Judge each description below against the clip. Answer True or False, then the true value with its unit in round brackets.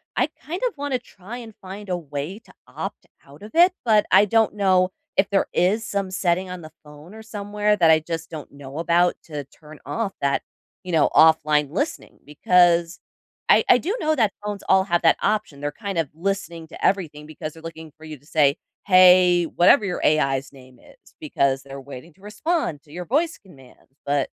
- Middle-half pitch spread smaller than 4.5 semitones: False (5.2 semitones)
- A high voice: False (175 Hz)